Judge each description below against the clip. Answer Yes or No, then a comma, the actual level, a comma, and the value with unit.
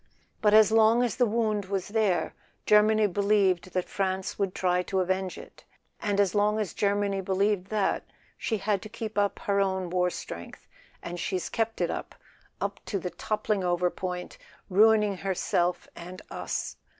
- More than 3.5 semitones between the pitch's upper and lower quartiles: No, narrow, 2.5 semitones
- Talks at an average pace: Yes, average, 165 wpm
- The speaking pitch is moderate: No, high, 200 Hz